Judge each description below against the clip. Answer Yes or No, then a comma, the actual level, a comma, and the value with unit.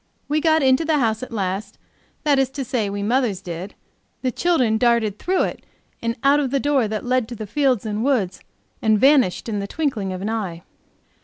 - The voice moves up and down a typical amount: Yes, average, 4.9 semitones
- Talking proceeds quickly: Yes, fast, 210 wpm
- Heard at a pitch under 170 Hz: No, high, 235 Hz